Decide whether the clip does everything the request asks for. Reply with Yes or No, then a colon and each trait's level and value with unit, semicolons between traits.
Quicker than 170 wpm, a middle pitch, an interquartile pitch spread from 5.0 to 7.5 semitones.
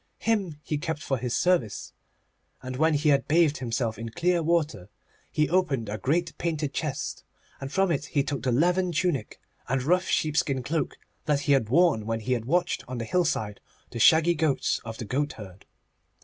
Yes: average, 185 wpm; medium, 145 Hz; wide, 5.5 semitones